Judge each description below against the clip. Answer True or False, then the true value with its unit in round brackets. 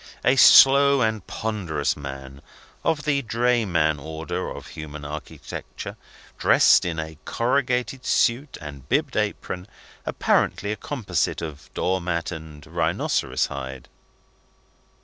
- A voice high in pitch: False (85 Hz)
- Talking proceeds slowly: True (115 wpm)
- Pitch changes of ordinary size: False (7.8 semitones)